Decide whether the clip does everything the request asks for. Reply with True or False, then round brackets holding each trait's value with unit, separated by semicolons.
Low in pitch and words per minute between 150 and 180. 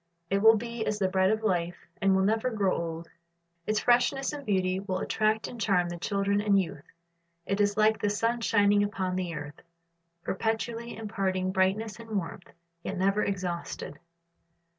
False (200 Hz; 170 wpm)